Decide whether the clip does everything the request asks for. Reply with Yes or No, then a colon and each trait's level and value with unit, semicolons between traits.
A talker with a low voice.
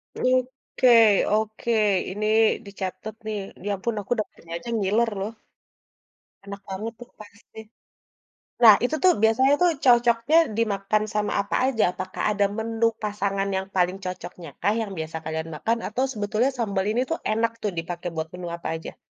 No: high, 210 Hz